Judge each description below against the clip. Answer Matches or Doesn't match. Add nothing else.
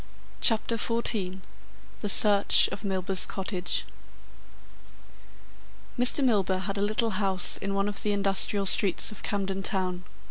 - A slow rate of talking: Matches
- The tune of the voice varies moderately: Doesn't match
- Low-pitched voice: Doesn't match